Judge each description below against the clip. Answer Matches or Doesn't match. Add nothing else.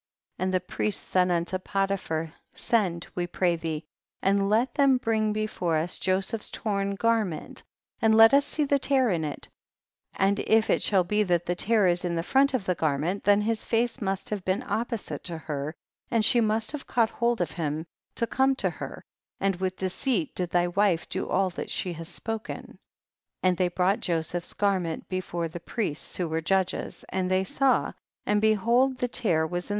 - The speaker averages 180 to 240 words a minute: Matches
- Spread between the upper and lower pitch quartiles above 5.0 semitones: Doesn't match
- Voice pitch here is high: Matches